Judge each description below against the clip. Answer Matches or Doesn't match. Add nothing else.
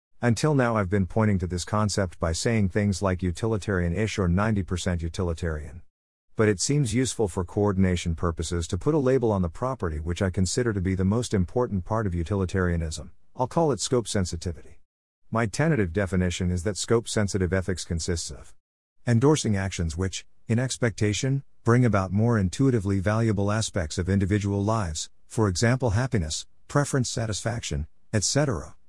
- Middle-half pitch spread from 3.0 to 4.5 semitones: Matches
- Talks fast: Doesn't match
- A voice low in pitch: Matches